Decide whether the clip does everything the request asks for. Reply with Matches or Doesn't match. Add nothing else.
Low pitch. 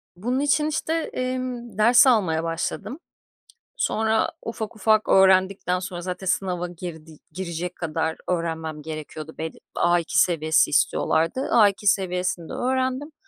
Doesn't match